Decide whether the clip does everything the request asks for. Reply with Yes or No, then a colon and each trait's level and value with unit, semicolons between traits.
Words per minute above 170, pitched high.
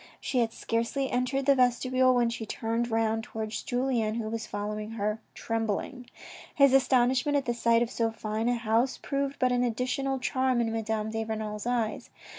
Yes: average, 180 wpm; high, 235 Hz